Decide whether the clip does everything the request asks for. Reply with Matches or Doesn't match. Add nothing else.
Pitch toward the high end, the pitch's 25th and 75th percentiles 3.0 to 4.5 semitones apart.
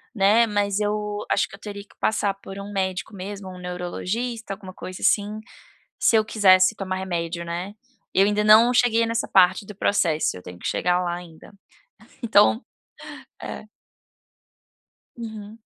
Doesn't match